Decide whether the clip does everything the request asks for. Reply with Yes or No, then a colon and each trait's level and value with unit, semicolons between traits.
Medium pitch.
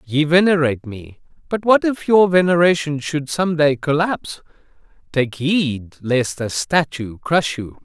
Yes: medium, 150 Hz